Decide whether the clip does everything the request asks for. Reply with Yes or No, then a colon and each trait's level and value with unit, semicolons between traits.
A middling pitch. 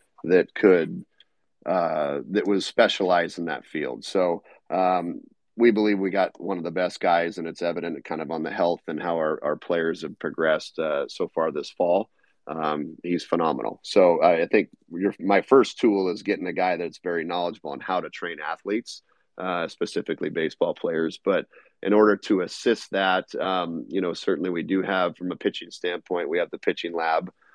No: very low, 90 Hz